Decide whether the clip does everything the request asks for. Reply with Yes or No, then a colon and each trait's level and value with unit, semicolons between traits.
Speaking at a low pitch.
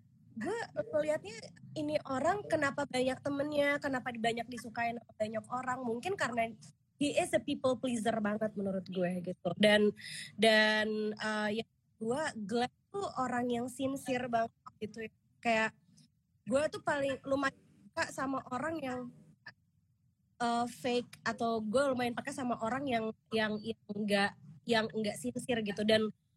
No: high, 235 Hz